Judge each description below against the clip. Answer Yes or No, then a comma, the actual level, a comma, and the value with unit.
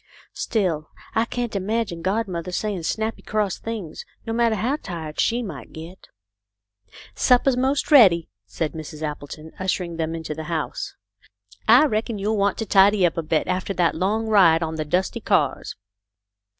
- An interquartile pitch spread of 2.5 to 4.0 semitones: No, wide, 5.5 semitones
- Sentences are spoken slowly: No, average, 175 wpm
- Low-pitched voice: No, medium, 185 Hz